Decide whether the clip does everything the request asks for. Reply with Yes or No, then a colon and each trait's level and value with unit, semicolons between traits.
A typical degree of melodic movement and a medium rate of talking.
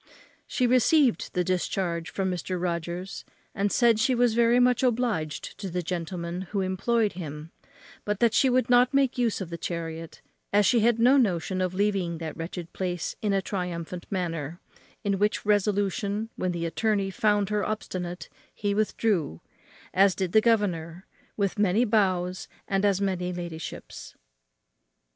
Yes: average, 3.7 semitones; average, 155 wpm